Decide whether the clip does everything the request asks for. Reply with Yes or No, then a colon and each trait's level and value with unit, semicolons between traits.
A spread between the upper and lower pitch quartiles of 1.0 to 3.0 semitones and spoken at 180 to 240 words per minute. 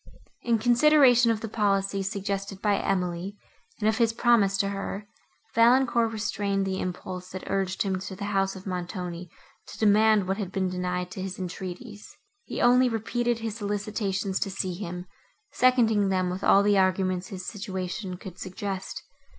No: narrow, 2.6 semitones; average, 165 wpm